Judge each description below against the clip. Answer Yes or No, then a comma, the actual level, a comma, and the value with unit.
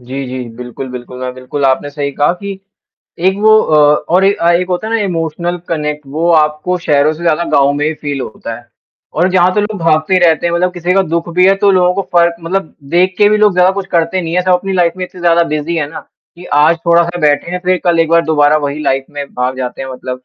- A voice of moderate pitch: Yes, medium, 170 Hz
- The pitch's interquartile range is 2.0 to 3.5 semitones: No, average, 3.9 semitones